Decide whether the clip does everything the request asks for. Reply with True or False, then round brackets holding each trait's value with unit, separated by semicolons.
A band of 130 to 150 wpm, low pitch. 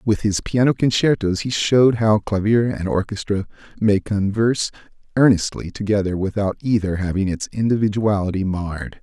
True (135 wpm; 105 Hz)